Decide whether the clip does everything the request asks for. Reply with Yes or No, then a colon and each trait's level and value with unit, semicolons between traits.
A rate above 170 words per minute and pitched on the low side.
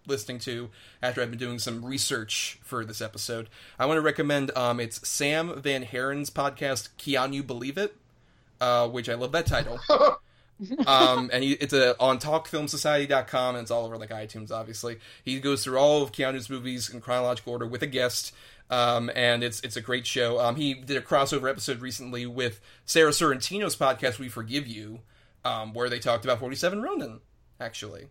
Yes: average, 185 wpm; low, 125 Hz